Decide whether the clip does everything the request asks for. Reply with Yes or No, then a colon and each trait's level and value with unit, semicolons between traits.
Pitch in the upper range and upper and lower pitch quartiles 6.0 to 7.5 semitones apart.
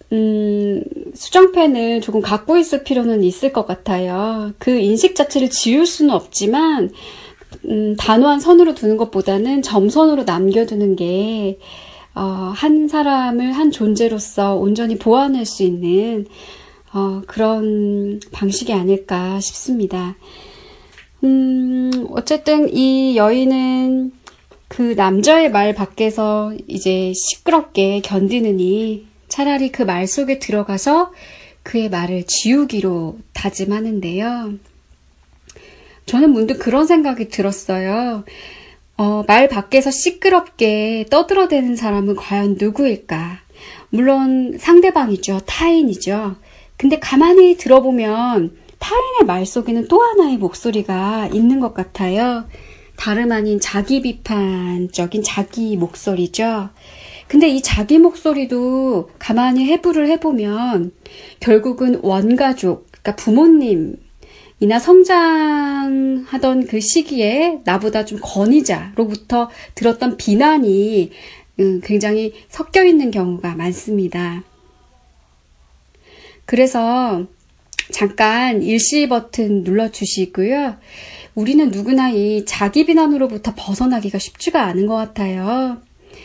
No: high, 225 Hz; wide, 5.4 semitones